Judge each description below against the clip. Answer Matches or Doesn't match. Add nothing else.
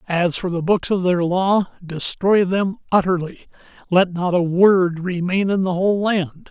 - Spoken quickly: Doesn't match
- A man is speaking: Matches